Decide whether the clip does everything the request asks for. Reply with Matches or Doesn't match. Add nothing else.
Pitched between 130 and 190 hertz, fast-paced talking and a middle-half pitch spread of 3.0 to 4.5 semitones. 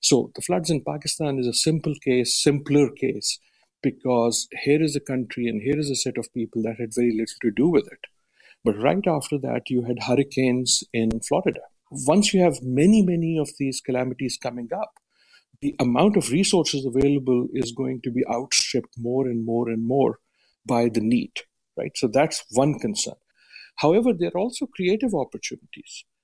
Doesn't match